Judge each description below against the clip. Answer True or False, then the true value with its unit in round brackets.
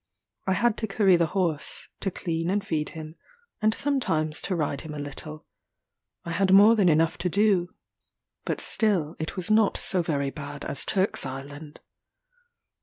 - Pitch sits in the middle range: True (170 Hz)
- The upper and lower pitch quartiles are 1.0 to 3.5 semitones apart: False (4.5 semitones)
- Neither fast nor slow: True (170 wpm)